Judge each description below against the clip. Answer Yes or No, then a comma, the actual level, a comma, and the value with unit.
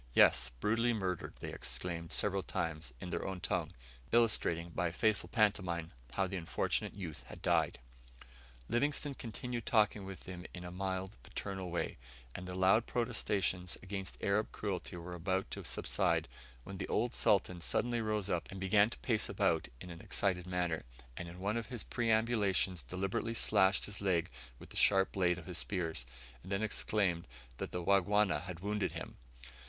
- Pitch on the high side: No, very low, 95 Hz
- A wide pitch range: No, average, 3.1 semitones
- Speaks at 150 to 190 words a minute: Yes, average, 170 wpm